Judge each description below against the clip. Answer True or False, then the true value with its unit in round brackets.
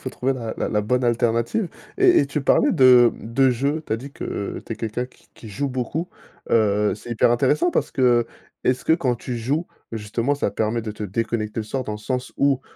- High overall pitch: False (120 Hz)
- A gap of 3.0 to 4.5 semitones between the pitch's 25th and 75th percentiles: True (3.3 semitones)